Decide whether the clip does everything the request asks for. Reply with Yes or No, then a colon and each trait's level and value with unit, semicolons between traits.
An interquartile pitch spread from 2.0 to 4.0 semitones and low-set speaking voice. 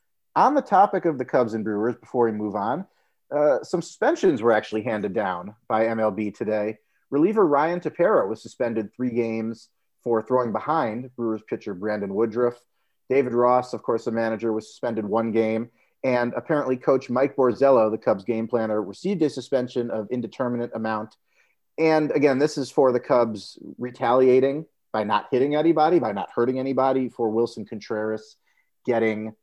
Yes: average, 2.9 semitones; low, 120 Hz